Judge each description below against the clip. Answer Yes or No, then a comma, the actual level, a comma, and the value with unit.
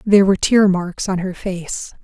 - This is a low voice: No, high, 190 Hz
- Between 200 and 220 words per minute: Yes, fast, 205 wpm